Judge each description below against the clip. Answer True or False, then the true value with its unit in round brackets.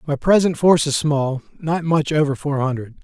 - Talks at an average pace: True (180 wpm)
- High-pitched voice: False (150 Hz)